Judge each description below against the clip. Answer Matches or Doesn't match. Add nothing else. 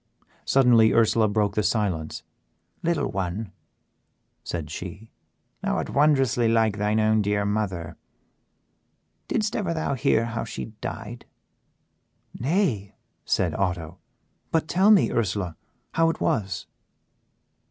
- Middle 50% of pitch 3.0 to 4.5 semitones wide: Doesn't match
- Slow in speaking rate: Matches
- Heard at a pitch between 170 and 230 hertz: Doesn't match